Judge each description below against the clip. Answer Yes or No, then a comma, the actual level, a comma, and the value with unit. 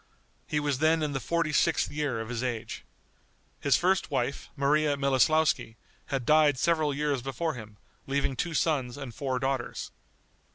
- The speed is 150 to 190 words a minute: Yes, average, 160 wpm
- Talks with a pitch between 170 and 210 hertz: No, medium, 140 Hz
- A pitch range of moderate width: Yes, average, 3.0 semitones